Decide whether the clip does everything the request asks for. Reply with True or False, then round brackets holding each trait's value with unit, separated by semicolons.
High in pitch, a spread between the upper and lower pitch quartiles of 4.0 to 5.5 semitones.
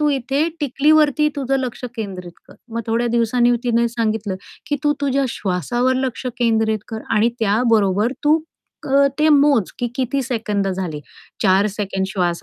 True (235 Hz; 4.6 semitones)